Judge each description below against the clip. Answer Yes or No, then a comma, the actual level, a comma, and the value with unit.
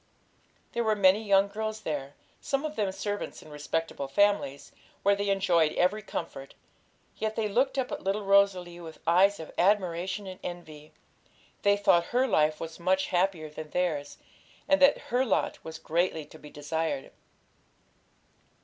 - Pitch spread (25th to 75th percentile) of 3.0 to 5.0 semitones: Yes, average, 4.2 semitones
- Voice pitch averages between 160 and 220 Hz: Yes, medium, 185 Hz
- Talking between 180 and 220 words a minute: No, average, 160 wpm